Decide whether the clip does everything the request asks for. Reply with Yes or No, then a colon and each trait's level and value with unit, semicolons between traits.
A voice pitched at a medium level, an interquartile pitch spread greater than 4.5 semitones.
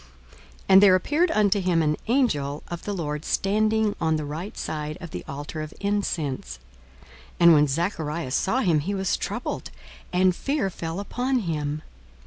Yes: medium, 175 Hz; average, 5.0 semitones